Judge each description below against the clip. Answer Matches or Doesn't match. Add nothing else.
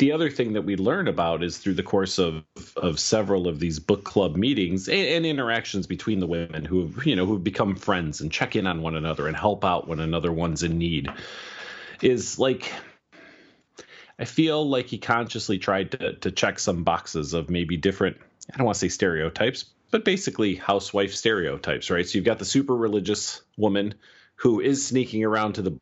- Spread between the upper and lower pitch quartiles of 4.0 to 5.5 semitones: Matches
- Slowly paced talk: Doesn't match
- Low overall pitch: Matches